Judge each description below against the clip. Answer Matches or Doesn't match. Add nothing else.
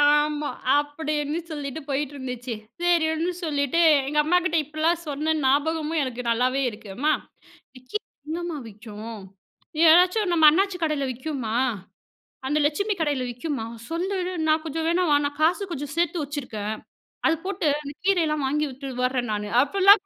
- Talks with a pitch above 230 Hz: Matches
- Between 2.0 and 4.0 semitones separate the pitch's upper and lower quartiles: Matches